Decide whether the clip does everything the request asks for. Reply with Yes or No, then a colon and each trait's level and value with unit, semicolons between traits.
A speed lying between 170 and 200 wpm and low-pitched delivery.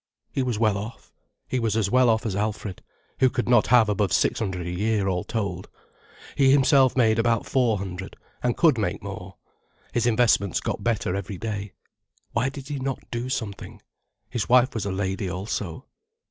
Yes: average, 185 wpm; low, 110 Hz